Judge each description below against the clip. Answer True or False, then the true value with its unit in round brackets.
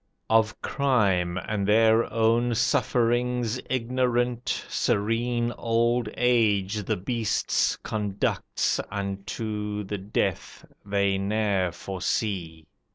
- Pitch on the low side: True (110 Hz)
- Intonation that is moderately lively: True (3.1 semitones)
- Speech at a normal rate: False (90 wpm)